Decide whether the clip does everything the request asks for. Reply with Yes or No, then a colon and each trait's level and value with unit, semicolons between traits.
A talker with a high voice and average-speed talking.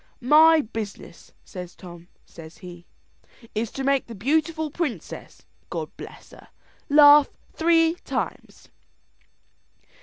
No: very high, 270 Hz; slow, 110 wpm